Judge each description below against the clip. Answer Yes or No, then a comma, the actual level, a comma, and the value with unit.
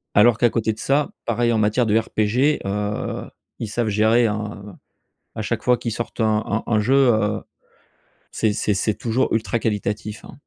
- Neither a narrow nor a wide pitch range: No, narrow, 2.0 semitones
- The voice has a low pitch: Yes, low, 110 Hz